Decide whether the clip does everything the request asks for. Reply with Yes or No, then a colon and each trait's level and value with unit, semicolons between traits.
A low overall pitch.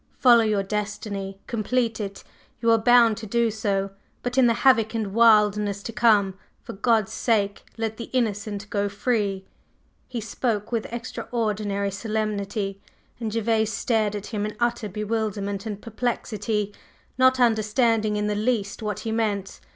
No: high, 215 Hz